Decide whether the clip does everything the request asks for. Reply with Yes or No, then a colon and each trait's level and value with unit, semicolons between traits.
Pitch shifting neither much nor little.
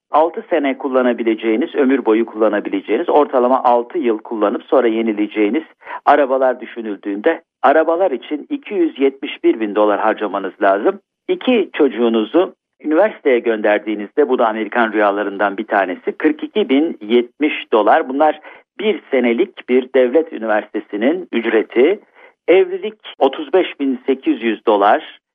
No: wide, 7.0 semitones